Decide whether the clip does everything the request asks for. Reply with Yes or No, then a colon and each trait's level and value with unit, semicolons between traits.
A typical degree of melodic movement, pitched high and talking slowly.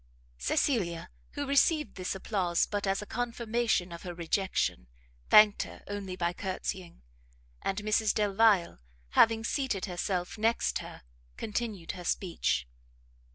Yes: average, 3.9 semitones; high, 200 Hz; slow, 125 wpm